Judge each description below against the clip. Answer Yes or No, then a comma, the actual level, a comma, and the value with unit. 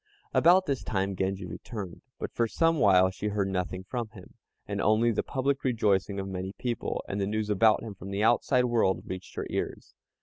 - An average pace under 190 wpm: No, average, 200 wpm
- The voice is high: No, low, 105 Hz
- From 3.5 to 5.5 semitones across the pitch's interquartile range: Yes, average, 3.8 semitones